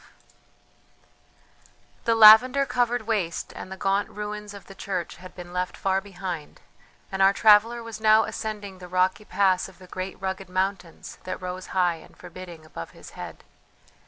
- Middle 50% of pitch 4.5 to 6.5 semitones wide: No, narrow, 2.6 semitones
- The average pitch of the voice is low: No, high, 195 Hz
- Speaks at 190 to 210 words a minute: No, average, 165 wpm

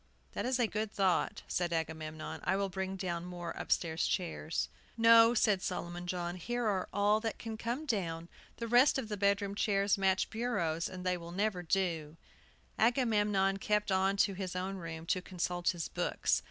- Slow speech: No, average, 180 wpm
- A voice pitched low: No, high, 190 Hz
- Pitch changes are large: No, average, 3.4 semitones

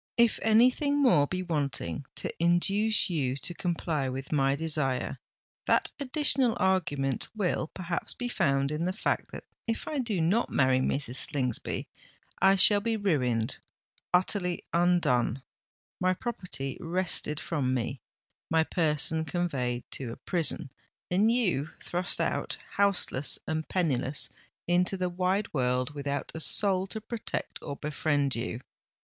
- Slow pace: Yes, slow, 130 wpm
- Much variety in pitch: Yes, wide, 5.9 semitones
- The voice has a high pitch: No, medium, 165 Hz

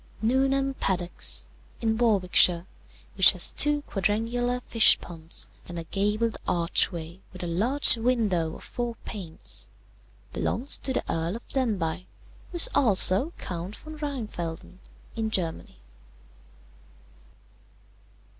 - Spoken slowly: Yes, slow, 115 wpm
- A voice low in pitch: No, high, 210 Hz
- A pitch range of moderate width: No, wide, 5.8 semitones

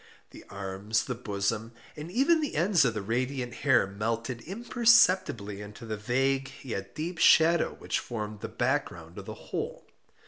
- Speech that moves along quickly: No, average, 165 wpm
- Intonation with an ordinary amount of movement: No, wide, 7.0 semitones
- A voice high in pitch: No, low, 120 Hz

